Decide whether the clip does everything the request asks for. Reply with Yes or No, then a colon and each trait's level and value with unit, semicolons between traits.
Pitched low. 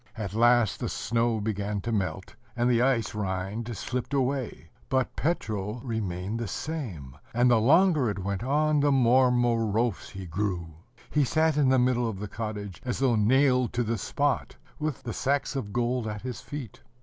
Yes: low, 120 Hz